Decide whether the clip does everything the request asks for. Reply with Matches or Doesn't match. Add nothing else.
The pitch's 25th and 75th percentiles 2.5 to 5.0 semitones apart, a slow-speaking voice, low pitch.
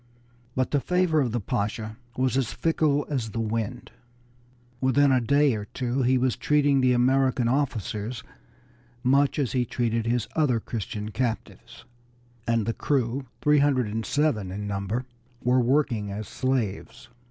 Doesn't match